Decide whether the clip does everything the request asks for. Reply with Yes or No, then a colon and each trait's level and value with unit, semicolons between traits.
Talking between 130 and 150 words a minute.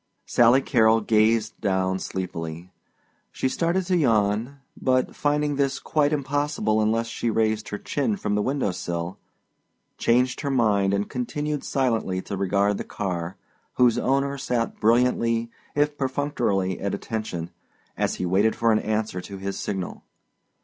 Yes: average, 145 wpm